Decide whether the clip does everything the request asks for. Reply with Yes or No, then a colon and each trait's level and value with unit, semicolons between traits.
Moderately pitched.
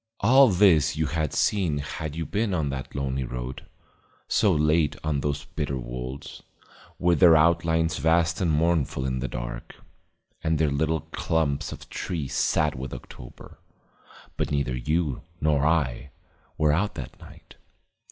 No: very low, 75 Hz